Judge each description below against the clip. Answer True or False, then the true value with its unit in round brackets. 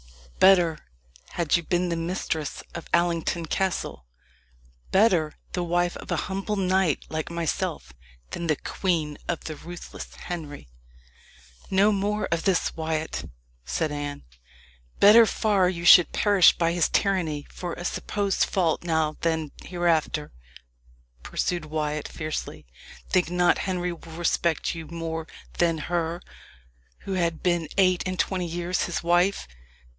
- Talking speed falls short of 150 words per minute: True (135 wpm)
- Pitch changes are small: True (2.3 semitones)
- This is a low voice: False (170 Hz)